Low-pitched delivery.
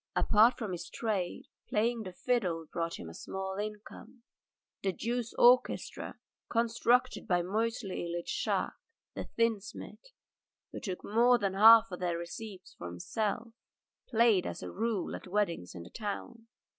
No: high, 210 Hz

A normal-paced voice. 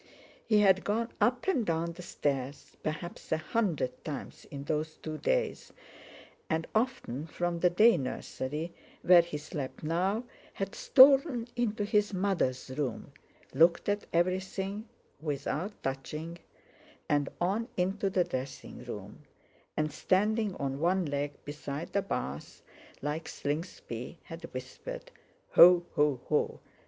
No: slow, 130 wpm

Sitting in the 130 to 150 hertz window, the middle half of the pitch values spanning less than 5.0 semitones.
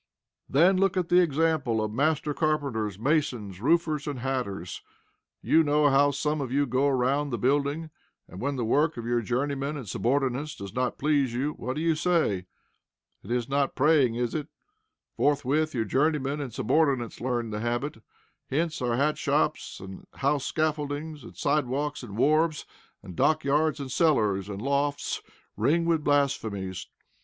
Yes: medium, 140 Hz; average, 3.9 semitones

